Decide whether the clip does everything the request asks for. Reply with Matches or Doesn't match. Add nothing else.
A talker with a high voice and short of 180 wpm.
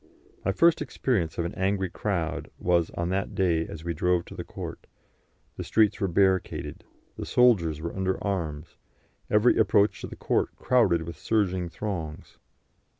Doesn't match